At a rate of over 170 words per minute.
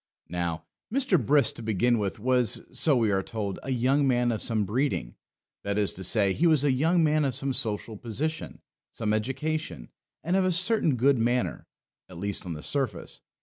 Yes: average, 190 wpm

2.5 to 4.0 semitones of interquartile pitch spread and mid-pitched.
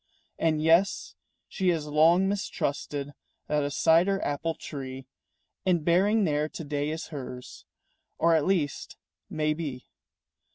Yes: average, 2.9 semitones; medium, 155 Hz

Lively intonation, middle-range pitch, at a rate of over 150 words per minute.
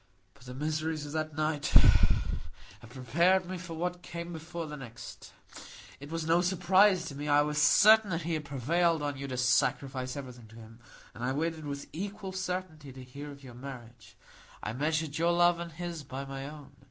No: average, 3.9 semitones; medium, 150 Hz; average, 195 wpm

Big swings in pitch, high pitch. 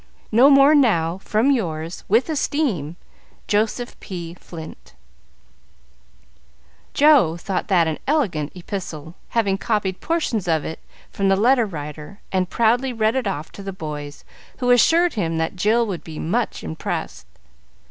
Yes: wide, 6.9 semitones; high, 195 Hz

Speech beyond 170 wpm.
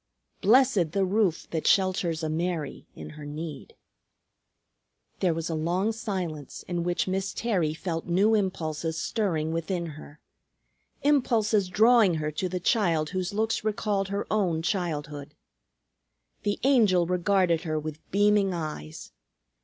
No: slow, 135 wpm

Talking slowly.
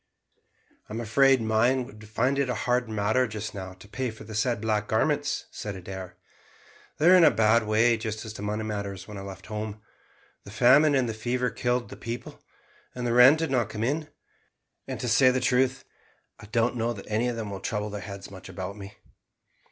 No: fast, 205 wpm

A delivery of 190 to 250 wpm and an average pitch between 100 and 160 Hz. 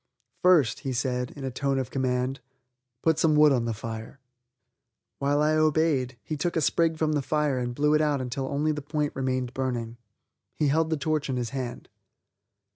Yes: average, 195 wpm; medium, 140 Hz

